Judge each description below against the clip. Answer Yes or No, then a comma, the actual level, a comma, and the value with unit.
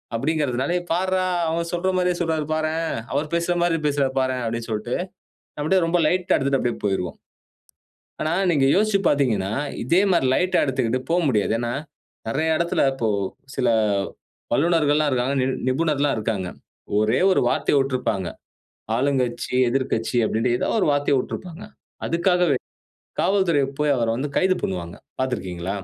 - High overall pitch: No, medium, 140 Hz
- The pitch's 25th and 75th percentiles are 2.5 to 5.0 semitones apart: No, wide, 5.5 semitones